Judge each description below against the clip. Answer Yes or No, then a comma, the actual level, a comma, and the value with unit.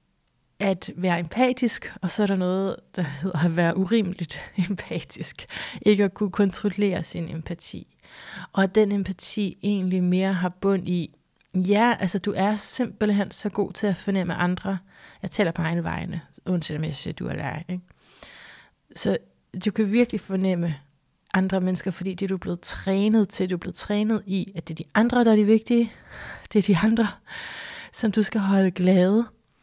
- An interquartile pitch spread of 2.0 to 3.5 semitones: Yes, narrow, 2.5 semitones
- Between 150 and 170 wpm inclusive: No, average, 180 wpm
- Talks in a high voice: Yes, high, 195 Hz